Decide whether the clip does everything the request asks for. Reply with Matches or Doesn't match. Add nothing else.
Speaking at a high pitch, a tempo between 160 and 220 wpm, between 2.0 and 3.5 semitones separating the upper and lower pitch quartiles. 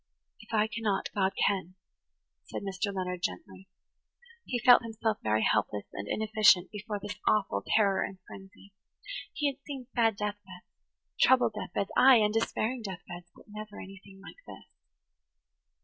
Doesn't match